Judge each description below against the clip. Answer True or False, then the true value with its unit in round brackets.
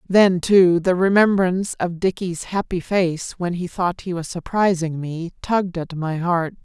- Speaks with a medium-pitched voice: True (180 Hz)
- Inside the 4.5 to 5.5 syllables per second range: False (4.3 syllables/s)